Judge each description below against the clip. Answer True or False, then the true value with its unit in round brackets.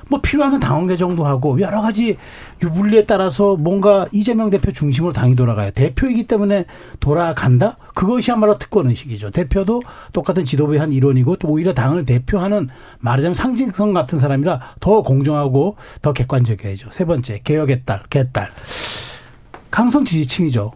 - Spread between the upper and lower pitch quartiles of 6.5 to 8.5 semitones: True (7.4 semitones)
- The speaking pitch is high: False (170 Hz)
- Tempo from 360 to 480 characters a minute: True (375 characters per minute)